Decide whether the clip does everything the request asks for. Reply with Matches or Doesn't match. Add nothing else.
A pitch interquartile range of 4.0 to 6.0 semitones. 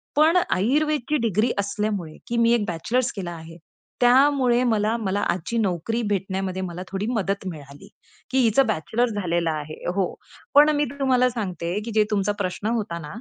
Matches